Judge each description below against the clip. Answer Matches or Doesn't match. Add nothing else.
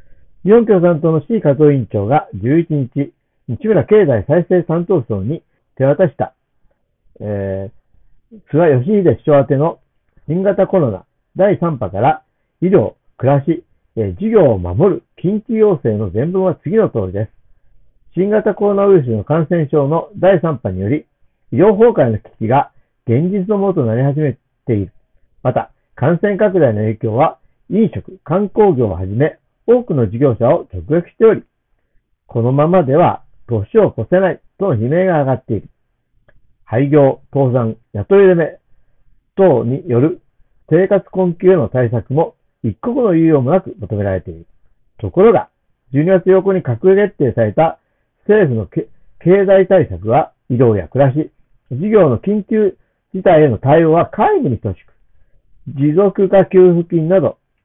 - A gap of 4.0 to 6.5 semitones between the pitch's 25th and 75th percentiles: Doesn't match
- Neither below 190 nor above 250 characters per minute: Doesn't match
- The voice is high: Doesn't match